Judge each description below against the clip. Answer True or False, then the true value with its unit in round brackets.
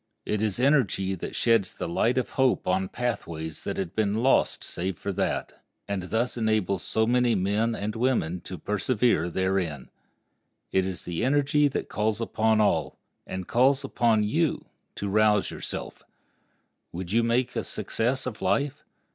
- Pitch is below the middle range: True (110 Hz)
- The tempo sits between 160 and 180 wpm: False (150 wpm)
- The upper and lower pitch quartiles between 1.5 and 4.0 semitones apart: False (4.4 semitones)